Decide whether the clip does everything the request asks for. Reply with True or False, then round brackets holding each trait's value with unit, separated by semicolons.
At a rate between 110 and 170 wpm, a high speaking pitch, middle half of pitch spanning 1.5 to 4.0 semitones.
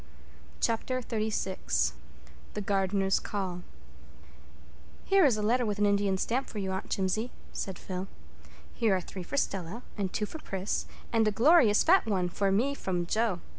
True (160 wpm; 205 Hz; 3.3 semitones)